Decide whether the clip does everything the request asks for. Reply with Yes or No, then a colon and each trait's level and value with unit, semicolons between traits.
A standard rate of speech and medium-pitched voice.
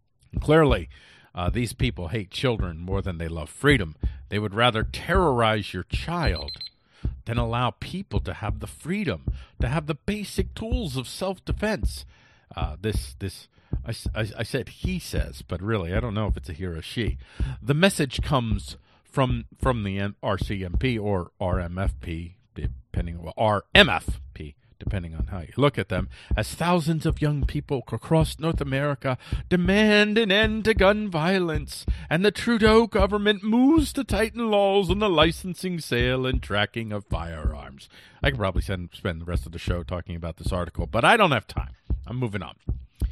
No: average, 170 wpm; low, 110 Hz